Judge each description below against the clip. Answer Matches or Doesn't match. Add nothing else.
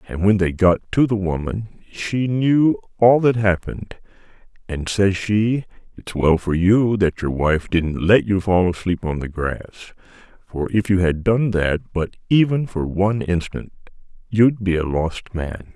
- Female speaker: Doesn't match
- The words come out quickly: Doesn't match